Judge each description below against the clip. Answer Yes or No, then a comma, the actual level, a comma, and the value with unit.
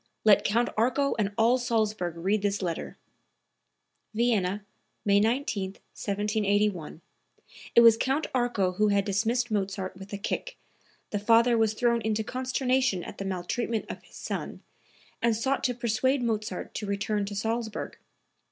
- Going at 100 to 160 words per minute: Yes, average, 145 wpm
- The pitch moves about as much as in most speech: Yes, average, 3.0 semitones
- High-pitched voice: Yes, high, 215 Hz